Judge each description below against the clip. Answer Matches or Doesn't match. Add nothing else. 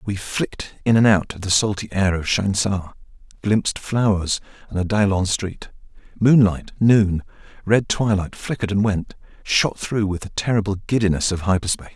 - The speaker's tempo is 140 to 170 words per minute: Matches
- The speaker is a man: Matches